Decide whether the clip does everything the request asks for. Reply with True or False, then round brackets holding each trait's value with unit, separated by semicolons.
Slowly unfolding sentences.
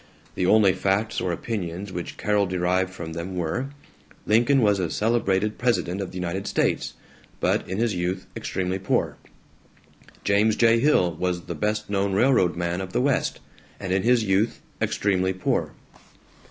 False (160 wpm)